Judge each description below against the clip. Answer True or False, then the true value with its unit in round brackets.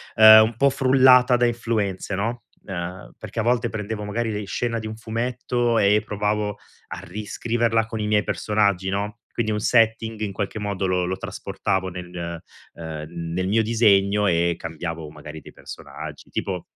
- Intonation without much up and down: False (3.3 semitones)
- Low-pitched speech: True (105 Hz)